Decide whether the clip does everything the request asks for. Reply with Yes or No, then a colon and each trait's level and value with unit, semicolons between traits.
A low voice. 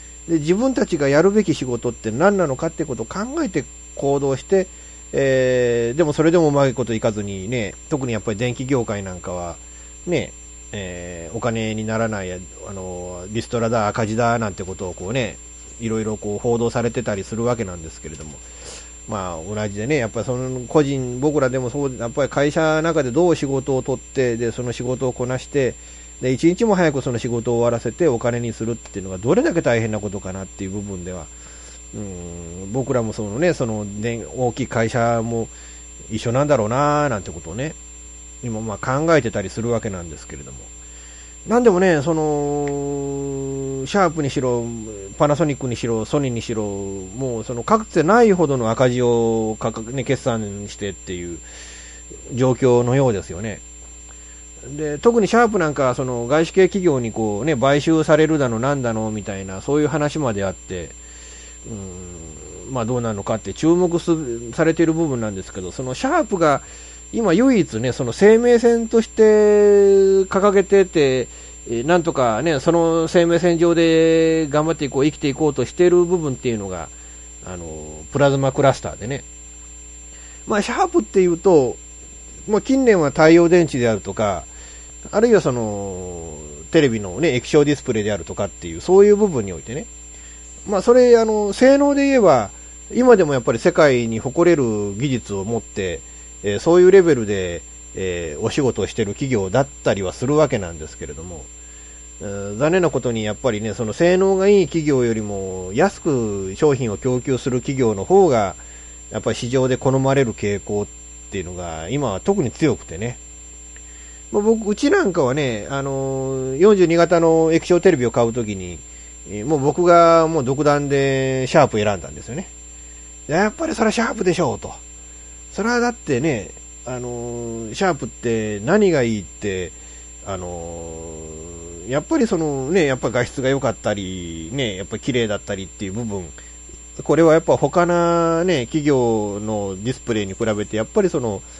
Yes: low, 120 Hz